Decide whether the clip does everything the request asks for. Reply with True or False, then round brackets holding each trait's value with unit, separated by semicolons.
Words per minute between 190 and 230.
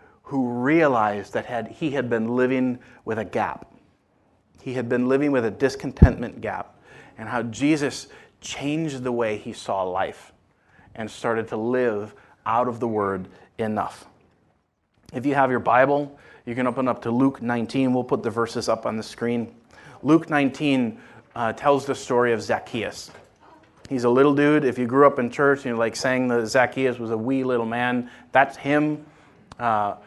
False (180 wpm)